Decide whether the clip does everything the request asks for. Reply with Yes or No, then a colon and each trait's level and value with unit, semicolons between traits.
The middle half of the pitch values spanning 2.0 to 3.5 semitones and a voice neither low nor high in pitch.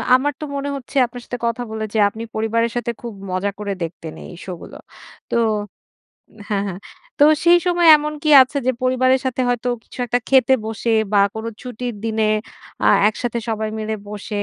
No: average, 2.9 semitones; high, 235 Hz